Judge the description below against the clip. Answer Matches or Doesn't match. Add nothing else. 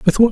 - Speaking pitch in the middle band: Doesn't match